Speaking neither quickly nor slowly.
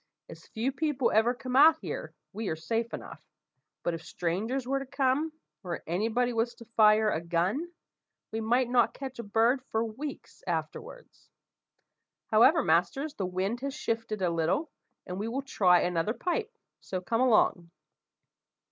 Yes: average, 165 wpm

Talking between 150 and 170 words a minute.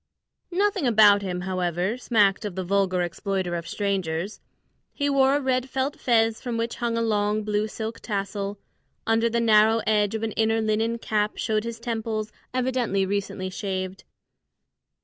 Yes: average, 160 wpm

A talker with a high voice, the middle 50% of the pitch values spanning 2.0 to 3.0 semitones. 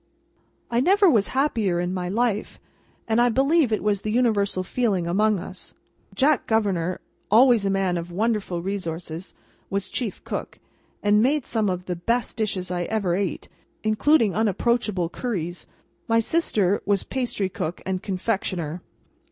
No: high, 205 Hz; average, 4.2 semitones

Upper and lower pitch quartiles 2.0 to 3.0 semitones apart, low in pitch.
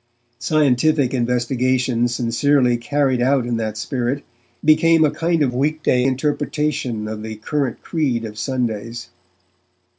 No: average, 3.6 semitones; low, 130 Hz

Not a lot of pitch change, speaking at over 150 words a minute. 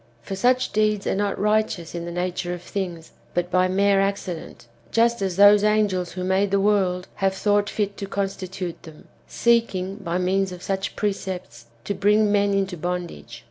Yes: narrow, 2.2 semitones; average, 180 wpm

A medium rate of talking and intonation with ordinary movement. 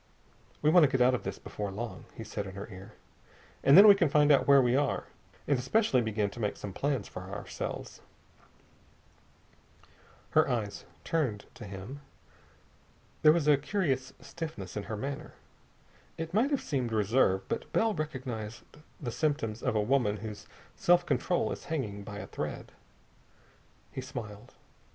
No: average, 165 wpm; wide, 6.1 semitones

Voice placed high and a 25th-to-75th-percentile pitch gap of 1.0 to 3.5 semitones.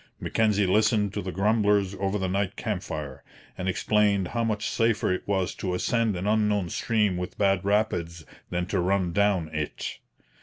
No: low, 100 Hz; narrow, 2.6 semitones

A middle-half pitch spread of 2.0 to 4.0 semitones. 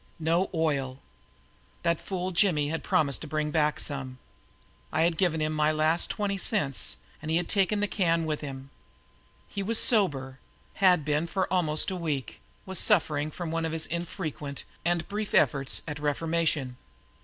Yes: average, 3.3 semitones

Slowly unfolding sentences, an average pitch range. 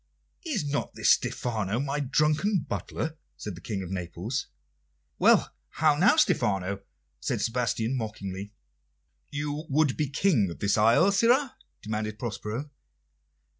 No: slow, 130 wpm; wide, 6.4 semitones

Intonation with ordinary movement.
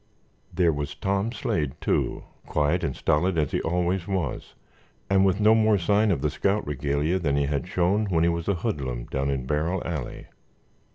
Yes: average, 5.0 semitones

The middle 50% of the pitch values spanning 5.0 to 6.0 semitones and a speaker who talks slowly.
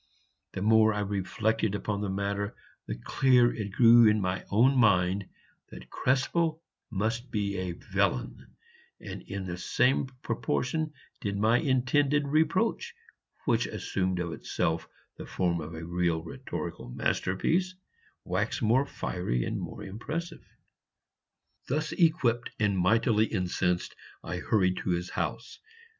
Yes: wide, 5.4 semitones; slow, 130 wpm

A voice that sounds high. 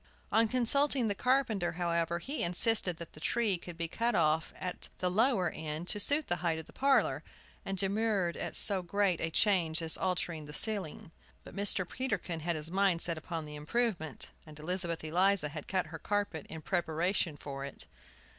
No: medium, 175 Hz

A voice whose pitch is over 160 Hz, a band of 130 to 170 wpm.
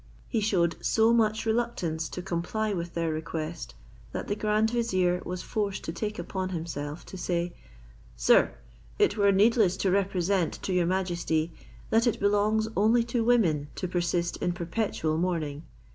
Yes: medium, 185 Hz; average, 160 wpm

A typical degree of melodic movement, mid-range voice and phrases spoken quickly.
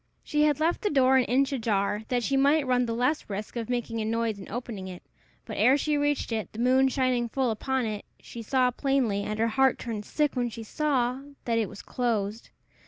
No: average, 3.3 semitones; high, 245 Hz; fast, 225 wpm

